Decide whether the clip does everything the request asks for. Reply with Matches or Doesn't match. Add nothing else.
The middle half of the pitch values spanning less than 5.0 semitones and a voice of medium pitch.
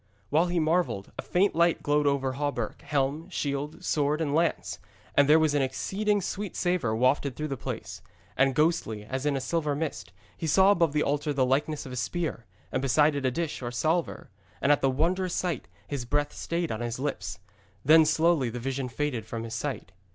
Matches